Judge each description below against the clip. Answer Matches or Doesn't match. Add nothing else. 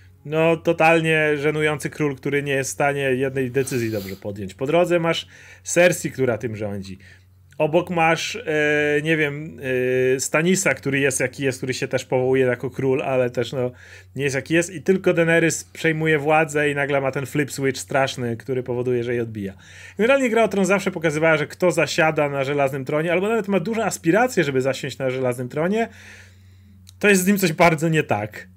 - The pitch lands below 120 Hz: Doesn't match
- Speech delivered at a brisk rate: Matches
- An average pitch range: Matches